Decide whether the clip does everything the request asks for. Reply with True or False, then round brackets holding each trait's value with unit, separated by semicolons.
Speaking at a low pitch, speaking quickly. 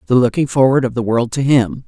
True (130 Hz; 255 wpm)